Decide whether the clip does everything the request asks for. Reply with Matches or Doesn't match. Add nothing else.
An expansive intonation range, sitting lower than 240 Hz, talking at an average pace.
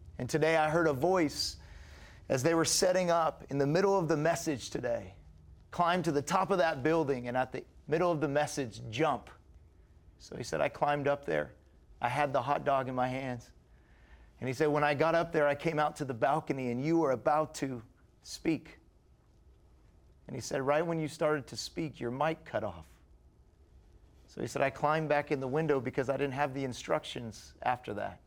Doesn't match